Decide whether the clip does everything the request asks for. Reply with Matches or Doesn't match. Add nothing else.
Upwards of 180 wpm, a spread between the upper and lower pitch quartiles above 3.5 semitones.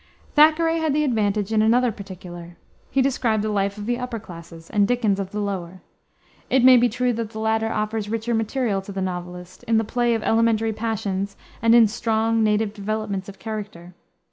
Doesn't match